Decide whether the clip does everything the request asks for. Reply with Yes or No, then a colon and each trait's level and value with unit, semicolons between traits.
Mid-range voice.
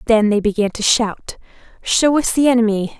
No: high, 225 Hz